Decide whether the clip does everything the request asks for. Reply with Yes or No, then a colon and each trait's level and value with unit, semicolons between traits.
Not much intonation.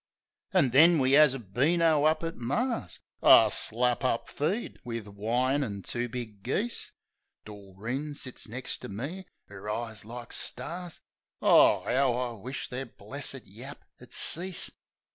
No: average, 5.0 semitones